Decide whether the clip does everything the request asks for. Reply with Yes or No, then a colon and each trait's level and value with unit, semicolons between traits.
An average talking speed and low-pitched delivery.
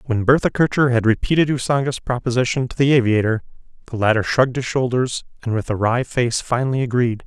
Yes: average, 180 wpm; low, 125 Hz